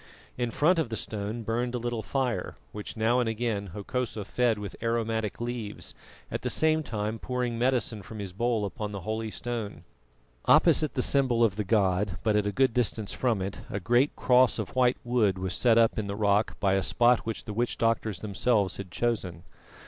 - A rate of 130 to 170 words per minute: No, average, 200 wpm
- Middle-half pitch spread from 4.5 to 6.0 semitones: No, average, 2.9 semitones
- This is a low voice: Yes, low, 115 Hz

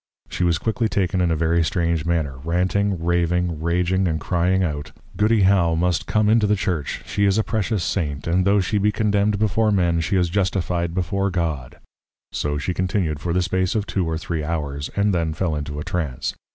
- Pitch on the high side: No, very low, 90 Hz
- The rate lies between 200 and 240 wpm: Yes, fast, 205 wpm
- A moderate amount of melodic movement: Yes, average, 3.3 semitones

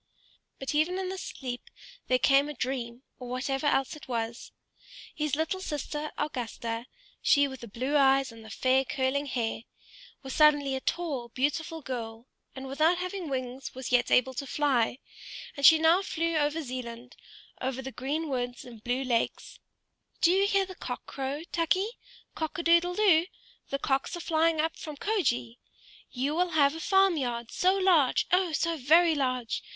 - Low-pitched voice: No, very high, 280 Hz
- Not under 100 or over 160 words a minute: No, average, 175 wpm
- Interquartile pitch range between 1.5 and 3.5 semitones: No, average, 4.4 semitones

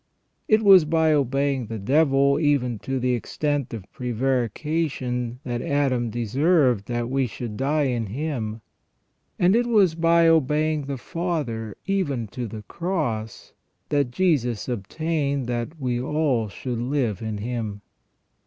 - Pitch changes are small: No, average, 4.6 semitones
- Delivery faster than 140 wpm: No, slow, 135 wpm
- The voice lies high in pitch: No, low, 135 Hz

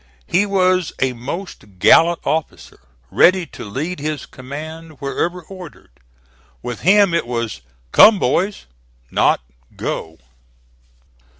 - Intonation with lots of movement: Yes, wide, 5.9 semitones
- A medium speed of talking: No, slow, 110 wpm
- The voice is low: No, medium, 160 Hz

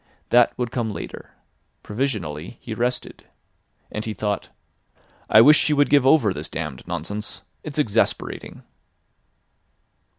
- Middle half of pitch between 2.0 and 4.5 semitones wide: Yes, average, 4.1 semitones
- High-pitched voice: No, low, 110 Hz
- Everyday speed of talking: No, slow, 125 wpm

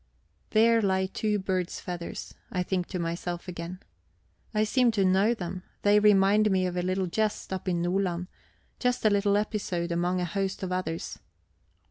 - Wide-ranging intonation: No, narrow, 2.6 semitones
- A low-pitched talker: No, high, 190 Hz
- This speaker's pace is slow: No, average, 170 wpm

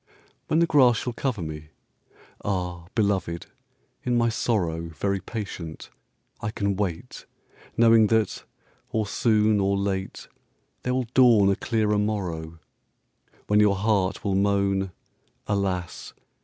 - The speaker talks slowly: Yes, slow, 105 wpm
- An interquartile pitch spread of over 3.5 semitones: No, average, 3.1 semitones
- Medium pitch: No, low, 100 Hz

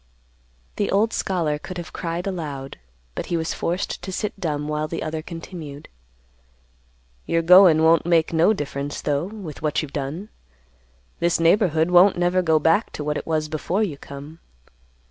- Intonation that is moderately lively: Yes, average, 3.0 semitones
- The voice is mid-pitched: Yes, medium, 165 Hz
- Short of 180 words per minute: Yes, average, 165 wpm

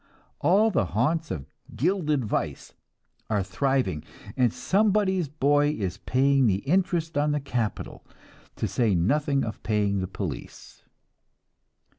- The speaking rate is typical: No, slow, 125 wpm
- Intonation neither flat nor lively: No, wide, 6.9 semitones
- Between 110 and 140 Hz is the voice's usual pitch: Yes, low, 135 Hz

